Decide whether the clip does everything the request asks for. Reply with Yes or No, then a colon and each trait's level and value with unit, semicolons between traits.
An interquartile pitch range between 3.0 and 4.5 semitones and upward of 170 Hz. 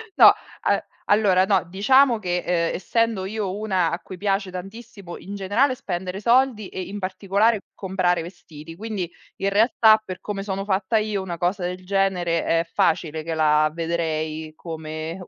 Yes: average, 3.3 semitones; high, 190 Hz